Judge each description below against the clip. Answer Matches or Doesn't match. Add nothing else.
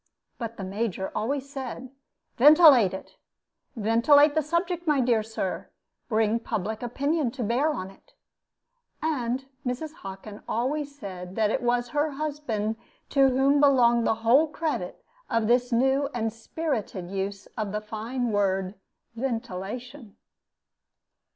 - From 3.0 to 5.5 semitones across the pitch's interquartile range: Matches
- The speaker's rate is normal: Doesn't match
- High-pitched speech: Matches